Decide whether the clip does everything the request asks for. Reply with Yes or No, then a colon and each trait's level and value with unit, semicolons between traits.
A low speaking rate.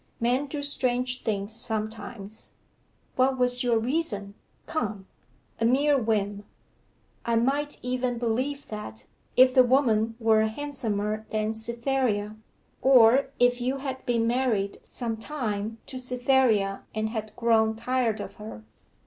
Yes: slow, 130 wpm